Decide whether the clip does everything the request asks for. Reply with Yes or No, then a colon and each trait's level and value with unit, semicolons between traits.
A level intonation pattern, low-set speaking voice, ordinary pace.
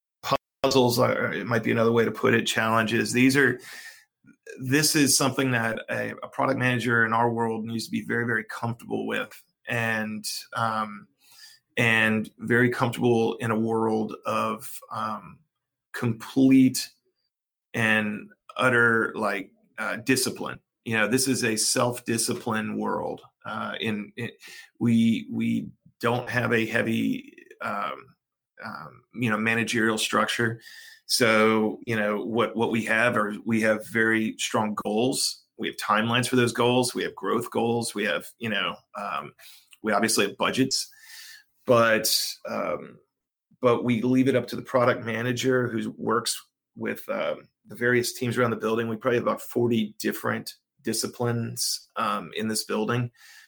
Yes: narrow, 2.2 semitones; low, 120 Hz; average, 150 wpm